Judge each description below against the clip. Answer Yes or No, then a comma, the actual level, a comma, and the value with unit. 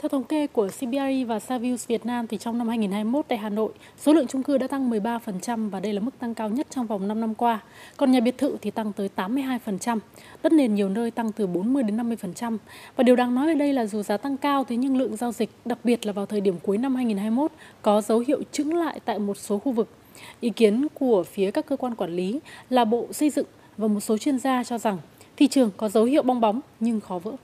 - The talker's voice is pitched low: No, high, 235 Hz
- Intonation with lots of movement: No, average, 3.7 semitones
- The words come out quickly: Yes, fast, 255 wpm